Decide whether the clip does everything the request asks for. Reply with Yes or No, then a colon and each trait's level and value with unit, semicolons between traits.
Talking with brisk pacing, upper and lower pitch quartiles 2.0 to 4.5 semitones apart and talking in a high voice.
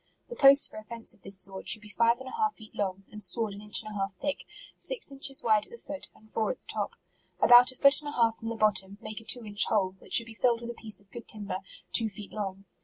Yes: fast, 290 wpm; average, 3.1 semitones; high, 220 Hz